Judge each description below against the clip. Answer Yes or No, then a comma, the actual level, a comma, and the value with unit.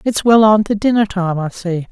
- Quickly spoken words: Yes, fast, 250 wpm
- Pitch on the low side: No, high, 200 Hz